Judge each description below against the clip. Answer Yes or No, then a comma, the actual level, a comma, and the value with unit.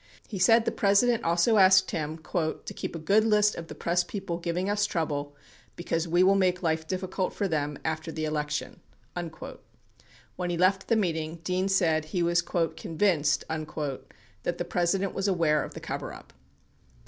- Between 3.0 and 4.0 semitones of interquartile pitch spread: Yes, average, 3.3 semitones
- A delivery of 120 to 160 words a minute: No, average, 170 wpm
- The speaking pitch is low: No, medium, 175 Hz